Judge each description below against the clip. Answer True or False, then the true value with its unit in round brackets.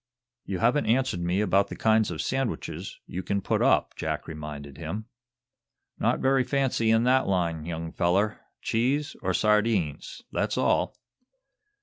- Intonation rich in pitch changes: True (5.7 semitones)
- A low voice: True (105 Hz)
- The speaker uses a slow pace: False (145 wpm)